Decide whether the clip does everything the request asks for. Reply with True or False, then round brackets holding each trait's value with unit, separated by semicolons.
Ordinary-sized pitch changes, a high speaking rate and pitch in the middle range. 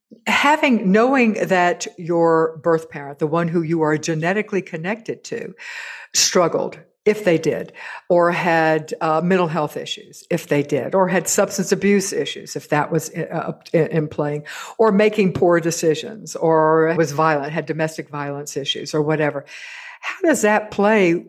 False (4.3 semitones; 160 wpm; 170 Hz)